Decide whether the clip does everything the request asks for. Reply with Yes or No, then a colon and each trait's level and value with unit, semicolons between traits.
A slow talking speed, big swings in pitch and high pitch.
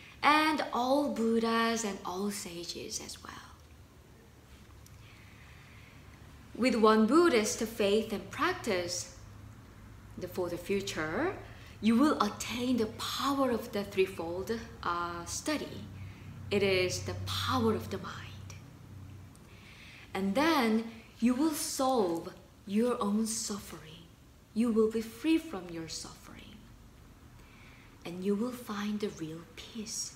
Yes: slow, 110 wpm; wide, 6.5 semitones; high, 205 Hz